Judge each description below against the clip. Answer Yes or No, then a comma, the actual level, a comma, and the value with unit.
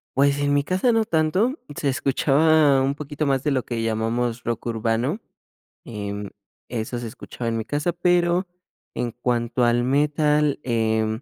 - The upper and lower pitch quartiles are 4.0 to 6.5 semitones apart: Yes, average, 4.3 semitones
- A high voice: No, low, 135 Hz